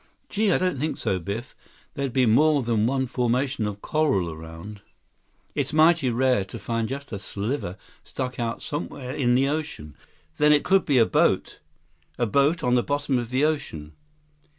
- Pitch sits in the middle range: No, low, 130 Hz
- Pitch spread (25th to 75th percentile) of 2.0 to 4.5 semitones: No, average, 4.9 semitones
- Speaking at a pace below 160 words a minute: No, average, 175 wpm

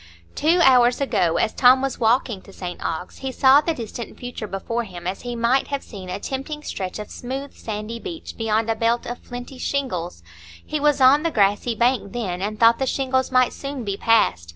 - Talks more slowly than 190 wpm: No, fast, 205 wpm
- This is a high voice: Yes, high, 240 Hz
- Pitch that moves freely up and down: No, average, 4.3 semitones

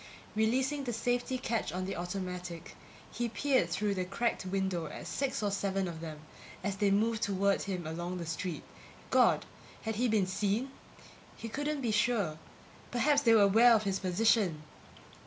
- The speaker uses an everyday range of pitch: Yes, average, 4.2 semitones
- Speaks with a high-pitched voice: Yes, high, 200 Hz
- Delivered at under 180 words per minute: Yes, average, 170 wpm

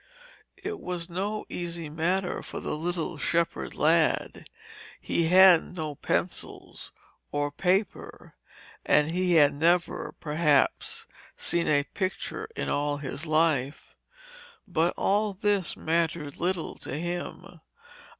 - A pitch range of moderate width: Yes, average, 3.0 semitones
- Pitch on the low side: No, medium, 170 Hz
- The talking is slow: Yes, slow, 115 wpm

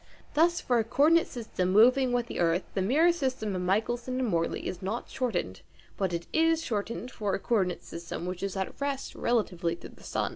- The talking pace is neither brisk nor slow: No, fast, 215 wpm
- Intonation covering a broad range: Yes, wide, 5.9 semitones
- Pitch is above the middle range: Yes, high, 220 Hz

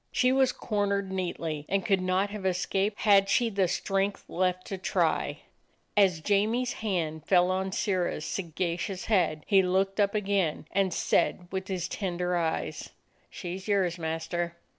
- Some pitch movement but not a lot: No, narrow, 2.1 semitones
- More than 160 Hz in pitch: Yes, high, 190 Hz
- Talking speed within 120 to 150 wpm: No, average, 160 wpm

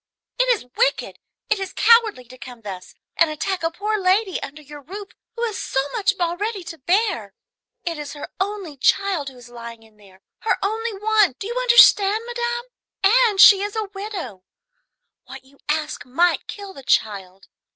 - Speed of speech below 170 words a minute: No, average, 180 wpm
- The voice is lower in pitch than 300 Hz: No, very high, 380 Hz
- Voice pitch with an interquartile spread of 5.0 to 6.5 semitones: No, wide, 8.0 semitones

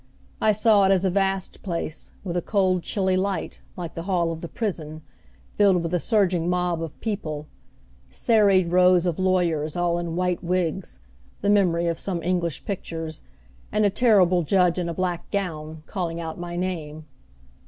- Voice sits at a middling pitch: Yes, medium, 180 Hz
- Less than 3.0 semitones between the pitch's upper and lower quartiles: Yes, narrow, 2.4 semitones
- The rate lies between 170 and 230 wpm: Yes, average, 175 wpm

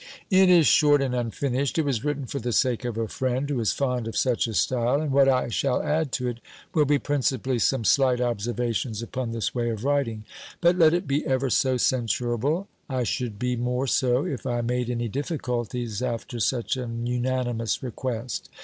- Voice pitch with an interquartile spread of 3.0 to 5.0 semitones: No, narrow, 2.6 semitones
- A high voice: No, low, 125 Hz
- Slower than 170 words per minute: No, average, 195 wpm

